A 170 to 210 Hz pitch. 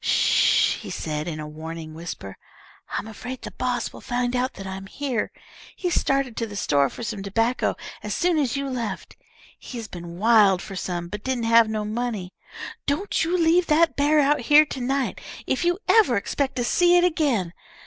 No: high, 240 Hz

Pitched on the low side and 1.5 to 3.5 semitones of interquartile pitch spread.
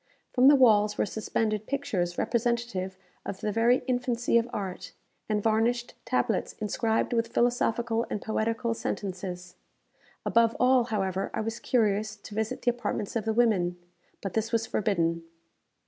No: high, 220 Hz; average, 2.7 semitones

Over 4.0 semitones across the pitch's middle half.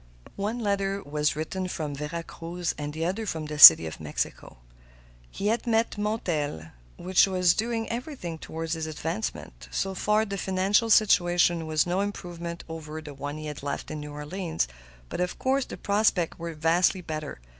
Yes: average, 4.5 semitones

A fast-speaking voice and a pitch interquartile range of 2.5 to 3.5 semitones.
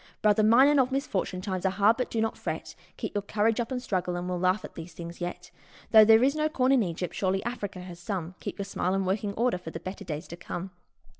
No: fast, 255 wpm; average, 4.0 semitones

